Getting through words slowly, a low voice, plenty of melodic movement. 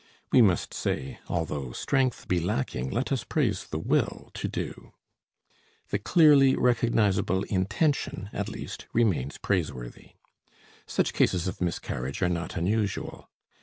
Yes: slow, 130 wpm; very low, 95 Hz; wide, 6.1 semitones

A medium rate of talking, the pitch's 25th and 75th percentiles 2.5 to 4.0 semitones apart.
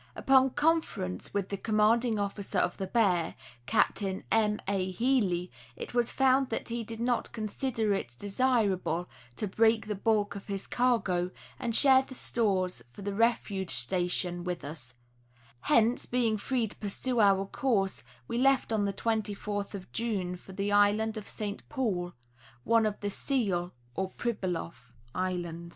Yes: average, 155 wpm; average, 3.7 semitones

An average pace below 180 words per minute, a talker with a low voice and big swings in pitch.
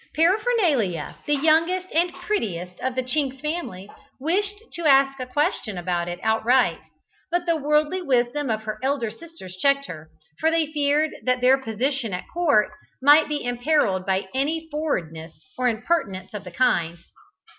No: average, 155 wpm; very high, 270 Hz; wide, 6.8 semitones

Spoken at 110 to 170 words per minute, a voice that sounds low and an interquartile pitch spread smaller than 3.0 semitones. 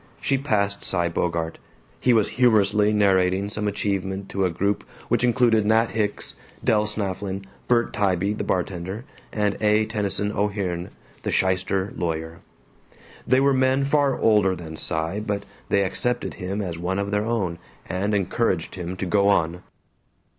Yes: average, 155 wpm; low, 100 Hz; narrow, 2.6 semitones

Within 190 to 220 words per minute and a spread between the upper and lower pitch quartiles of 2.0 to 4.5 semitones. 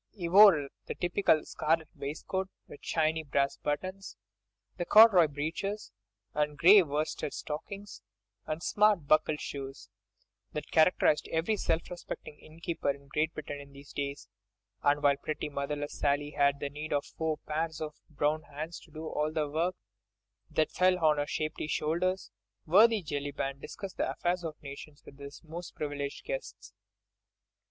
No: average, 145 wpm; average, 3.1 semitones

